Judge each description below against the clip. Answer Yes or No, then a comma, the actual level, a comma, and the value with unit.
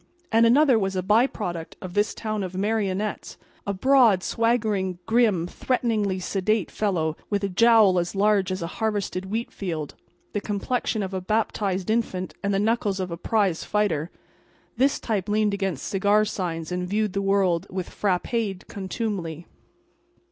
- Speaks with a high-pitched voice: Yes, high, 200 Hz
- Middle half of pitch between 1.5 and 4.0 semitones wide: Yes, average, 2.9 semitones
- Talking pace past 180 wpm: No, average, 155 wpm